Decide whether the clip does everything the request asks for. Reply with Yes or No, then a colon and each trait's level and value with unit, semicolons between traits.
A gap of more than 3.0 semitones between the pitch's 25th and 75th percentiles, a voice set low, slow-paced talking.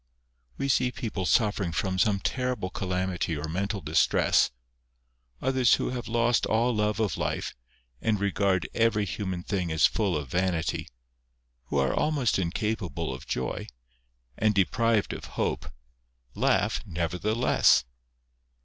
Yes: average, 4.4 semitones; low, 100 Hz; slow, 130 wpm